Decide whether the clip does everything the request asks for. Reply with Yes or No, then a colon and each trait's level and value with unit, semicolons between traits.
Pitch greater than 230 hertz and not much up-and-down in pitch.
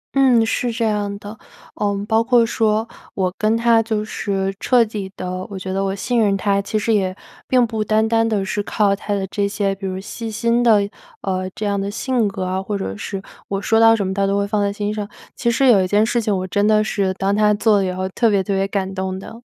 No: high, 205 Hz; narrow, 2.3 semitones